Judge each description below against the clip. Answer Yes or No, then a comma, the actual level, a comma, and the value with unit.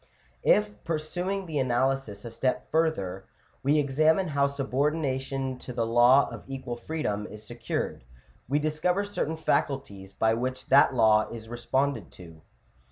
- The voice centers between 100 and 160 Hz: Yes, low, 135 Hz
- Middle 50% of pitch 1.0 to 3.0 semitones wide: No, average, 4.7 semitones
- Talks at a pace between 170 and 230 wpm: No, average, 145 wpm